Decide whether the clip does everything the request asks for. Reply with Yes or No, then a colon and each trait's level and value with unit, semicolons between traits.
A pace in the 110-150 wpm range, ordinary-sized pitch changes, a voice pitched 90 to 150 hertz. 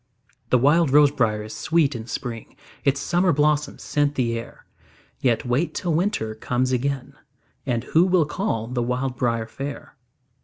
No: average, 160 wpm; average, 3.9 semitones; low, 135 Hz